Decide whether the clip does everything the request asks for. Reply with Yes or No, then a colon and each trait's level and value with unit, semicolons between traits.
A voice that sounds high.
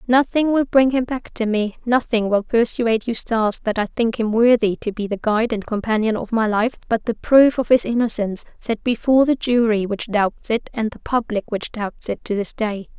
Yes: high, 225 Hz